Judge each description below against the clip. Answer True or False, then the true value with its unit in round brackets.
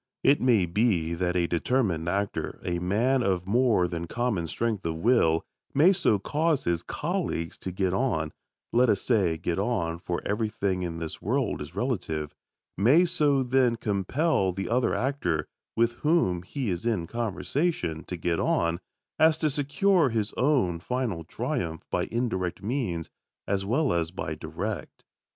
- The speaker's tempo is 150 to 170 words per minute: True (160 wpm)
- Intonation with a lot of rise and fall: True (6.9 semitones)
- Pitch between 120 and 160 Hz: False (100 Hz)